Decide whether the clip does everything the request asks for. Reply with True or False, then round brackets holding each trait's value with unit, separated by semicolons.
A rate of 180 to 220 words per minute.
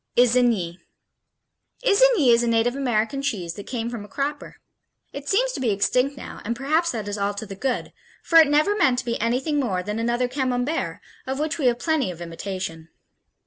True (190 wpm)